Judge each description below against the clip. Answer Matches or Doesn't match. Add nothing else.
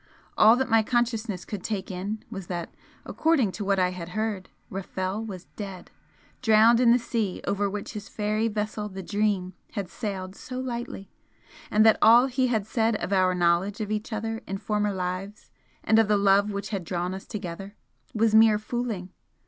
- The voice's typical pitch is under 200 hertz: Doesn't match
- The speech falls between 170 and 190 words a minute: Matches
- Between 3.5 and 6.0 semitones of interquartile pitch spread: Doesn't match